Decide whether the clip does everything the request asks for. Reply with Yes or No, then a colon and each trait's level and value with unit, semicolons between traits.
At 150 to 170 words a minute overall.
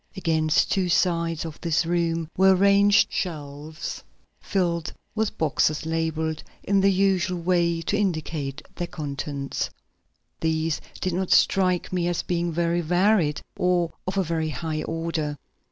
No: slow, 135 wpm